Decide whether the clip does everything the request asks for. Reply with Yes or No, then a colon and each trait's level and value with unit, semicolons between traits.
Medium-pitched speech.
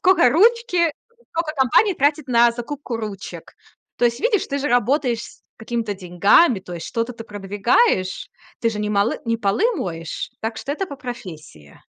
No: high, 235 Hz